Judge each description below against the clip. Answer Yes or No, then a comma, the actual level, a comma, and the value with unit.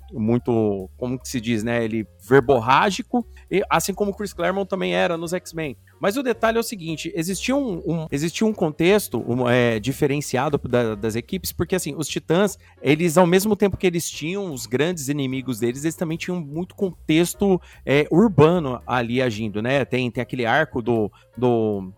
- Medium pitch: Yes, medium, 150 Hz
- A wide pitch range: Yes, wide, 7.0 semitones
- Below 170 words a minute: No, average, 180 wpm